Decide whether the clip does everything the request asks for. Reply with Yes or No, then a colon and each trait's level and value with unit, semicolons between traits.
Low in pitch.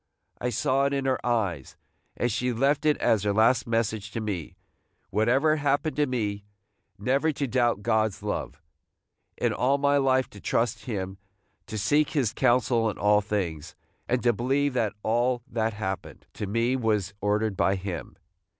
Yes: low, 115 Hz